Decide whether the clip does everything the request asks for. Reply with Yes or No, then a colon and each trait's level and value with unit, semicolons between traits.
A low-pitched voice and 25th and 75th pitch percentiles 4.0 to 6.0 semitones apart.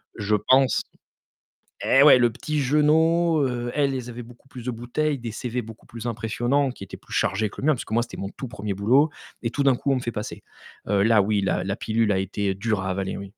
Yes: low, 120 Hz; average, 4.3 semitones